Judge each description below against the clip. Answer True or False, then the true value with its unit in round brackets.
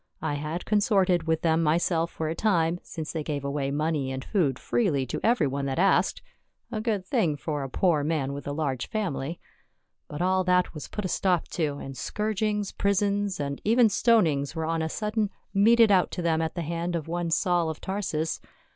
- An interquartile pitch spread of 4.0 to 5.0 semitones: True (4.7 semitones)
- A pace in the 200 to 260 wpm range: True (205 wpm)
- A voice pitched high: False (165 Hz)